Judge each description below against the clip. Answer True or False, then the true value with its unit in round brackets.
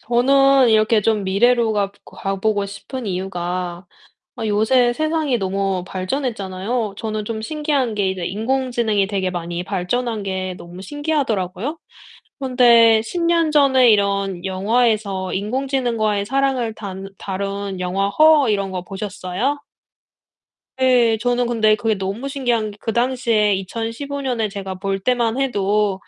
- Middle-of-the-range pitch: False (215 Hz)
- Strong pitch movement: False (4.2 semitones)